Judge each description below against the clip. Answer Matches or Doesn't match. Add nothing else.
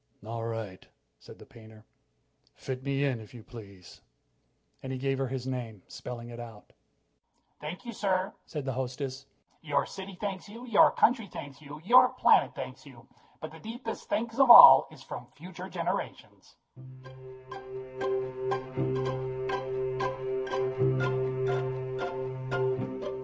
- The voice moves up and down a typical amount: Doesn't match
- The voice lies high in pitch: Doesn't match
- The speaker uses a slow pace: Matches